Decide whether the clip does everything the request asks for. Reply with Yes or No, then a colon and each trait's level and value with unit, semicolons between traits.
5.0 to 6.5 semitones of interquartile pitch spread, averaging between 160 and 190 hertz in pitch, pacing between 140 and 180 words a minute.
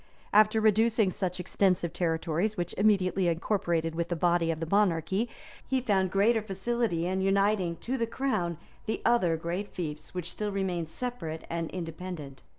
No: average, 4.0 semitones; medium, 185 Hz; average, 160 wpm